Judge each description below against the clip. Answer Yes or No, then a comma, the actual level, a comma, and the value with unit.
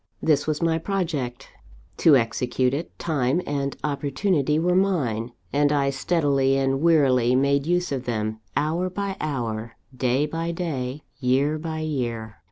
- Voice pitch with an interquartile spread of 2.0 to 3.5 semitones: No, average, 4.2 semitones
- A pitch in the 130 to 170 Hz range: Yes, medium, 140 Hz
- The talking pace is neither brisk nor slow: Yes, average, 145 wpm